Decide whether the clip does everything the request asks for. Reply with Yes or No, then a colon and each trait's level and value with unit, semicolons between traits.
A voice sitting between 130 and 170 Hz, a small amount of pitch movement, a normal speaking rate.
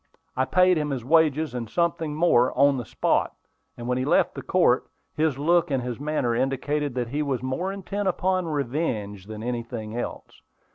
No: medium, 140 Hz; average, 4.7 semitones; average, 185 wpm